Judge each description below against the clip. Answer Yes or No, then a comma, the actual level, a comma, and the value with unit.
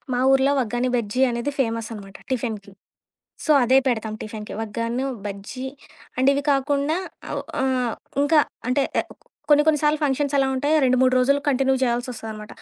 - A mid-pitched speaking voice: No, very high, 255 Hz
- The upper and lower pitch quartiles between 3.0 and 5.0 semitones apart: Yes, average, 3.6 semitones